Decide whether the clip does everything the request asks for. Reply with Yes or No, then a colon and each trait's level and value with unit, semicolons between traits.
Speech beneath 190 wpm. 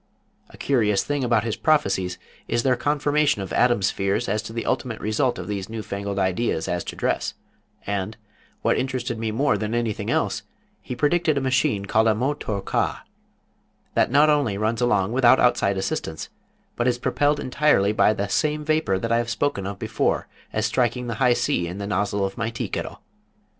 No: average, 195 wpm